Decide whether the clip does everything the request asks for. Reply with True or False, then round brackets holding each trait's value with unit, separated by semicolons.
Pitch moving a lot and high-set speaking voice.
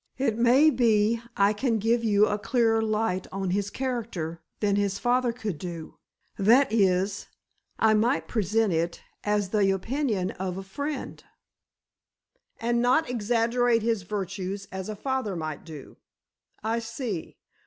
False (3.5 semitones; 215 Hz)